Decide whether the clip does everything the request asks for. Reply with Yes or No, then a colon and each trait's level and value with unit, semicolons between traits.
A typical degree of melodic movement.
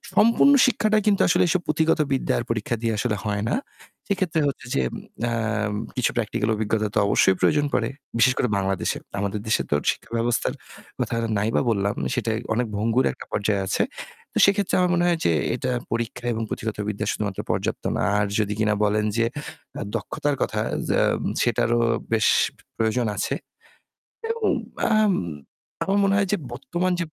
No: wide, 8.2 semitones